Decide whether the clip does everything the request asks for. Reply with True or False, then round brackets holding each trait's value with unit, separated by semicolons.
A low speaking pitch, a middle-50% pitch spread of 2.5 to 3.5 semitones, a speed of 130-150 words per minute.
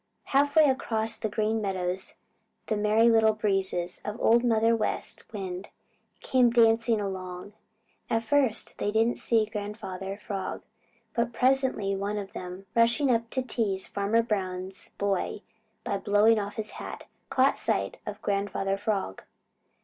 False (210 Hz; 2.8 semitones; 140 wpm)